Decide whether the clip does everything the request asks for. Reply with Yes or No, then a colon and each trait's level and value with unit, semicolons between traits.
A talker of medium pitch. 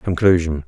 No: very low, 85 Hz